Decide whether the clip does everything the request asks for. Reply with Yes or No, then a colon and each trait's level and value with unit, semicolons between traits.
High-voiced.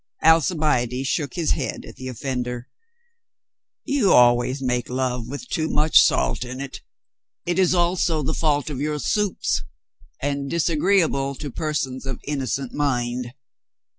No: medium, 140 Hz